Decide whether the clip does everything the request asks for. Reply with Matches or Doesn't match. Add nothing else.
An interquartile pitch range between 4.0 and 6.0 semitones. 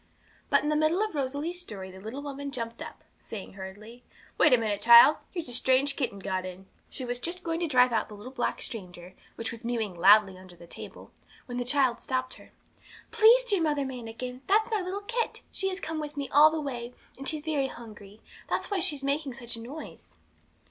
Matches